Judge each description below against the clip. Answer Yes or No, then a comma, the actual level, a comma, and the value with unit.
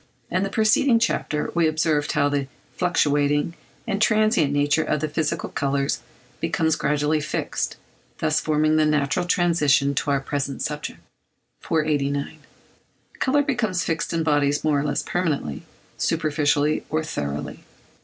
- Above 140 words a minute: No, slow, 135 wpm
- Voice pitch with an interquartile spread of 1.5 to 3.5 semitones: Yes, narrow, 2.6 semitones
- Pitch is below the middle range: No, medium, 150 Hz